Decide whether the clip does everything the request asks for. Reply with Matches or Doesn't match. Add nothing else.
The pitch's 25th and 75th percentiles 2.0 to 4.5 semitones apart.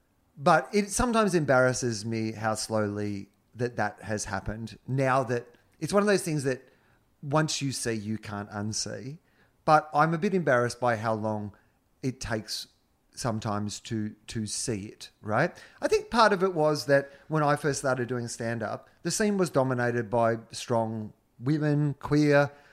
Doesn't match